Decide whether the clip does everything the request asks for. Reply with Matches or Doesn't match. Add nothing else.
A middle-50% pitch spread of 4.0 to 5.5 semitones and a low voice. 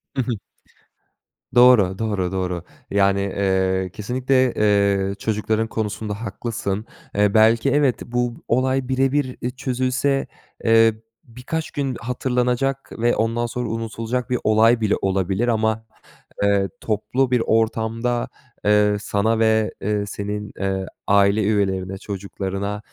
Doesn't match